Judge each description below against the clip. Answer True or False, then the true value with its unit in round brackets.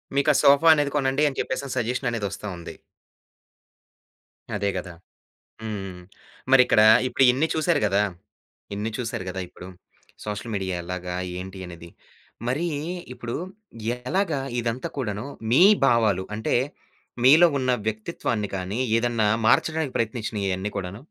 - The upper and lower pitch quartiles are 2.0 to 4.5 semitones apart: False (5.2 semitones)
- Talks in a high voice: False (115 Hz)